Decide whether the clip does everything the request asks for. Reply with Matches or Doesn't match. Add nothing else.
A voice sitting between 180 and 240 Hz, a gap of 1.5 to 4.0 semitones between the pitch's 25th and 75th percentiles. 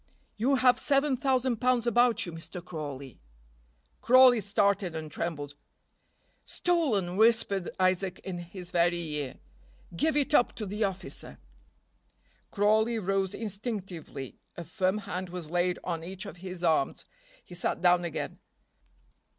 Doesn't match